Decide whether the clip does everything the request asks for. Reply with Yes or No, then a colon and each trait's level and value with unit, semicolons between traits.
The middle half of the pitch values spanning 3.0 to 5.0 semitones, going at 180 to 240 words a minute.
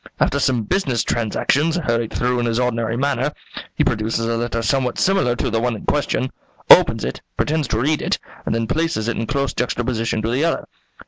Yes: average, 3.6 semitones; average, 200 wpm